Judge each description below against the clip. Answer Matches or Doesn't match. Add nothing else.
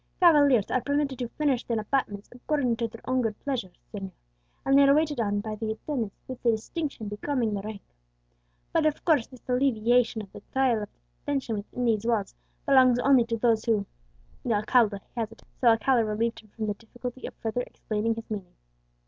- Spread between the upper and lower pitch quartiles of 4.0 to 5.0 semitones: Doesn't match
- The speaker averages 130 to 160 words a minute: Doesn't match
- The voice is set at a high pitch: Matches